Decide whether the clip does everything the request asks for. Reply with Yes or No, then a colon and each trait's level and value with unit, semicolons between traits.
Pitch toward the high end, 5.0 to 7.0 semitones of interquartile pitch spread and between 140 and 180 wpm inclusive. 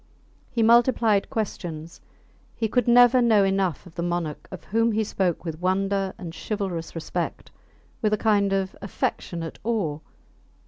No: high, 195 Hz; average, 4.1 semitones; average, 145 wpm